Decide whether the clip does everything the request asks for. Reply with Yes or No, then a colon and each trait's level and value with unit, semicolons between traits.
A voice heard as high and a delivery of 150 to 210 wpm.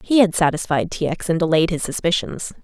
No: medium, 175 Hz; fast, 205 wpm